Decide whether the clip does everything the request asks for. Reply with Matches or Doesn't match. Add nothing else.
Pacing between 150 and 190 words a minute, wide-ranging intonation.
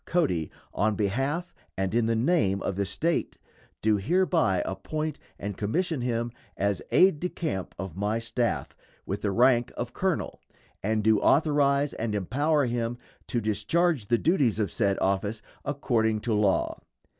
Matches